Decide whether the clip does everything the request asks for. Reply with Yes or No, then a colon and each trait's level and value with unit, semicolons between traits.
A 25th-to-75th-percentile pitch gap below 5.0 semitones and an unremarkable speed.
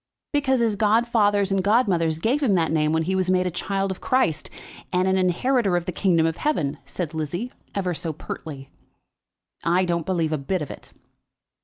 Yes: average, 4.0 semitones; average, 190 wpm